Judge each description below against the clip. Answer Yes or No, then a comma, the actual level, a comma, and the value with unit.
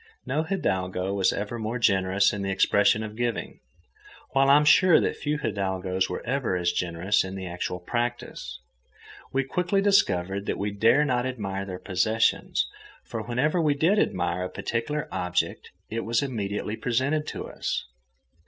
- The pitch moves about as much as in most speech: No, wide, 6.2 semitones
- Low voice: Yes, low, 110 Hz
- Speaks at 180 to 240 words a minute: No, average, 160 wpm